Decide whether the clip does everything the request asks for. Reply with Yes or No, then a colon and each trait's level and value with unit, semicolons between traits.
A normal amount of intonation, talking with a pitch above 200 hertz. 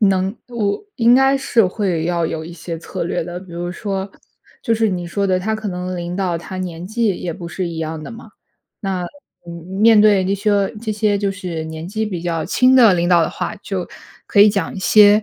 No: average, 3.5 semitones; high, 190 Hz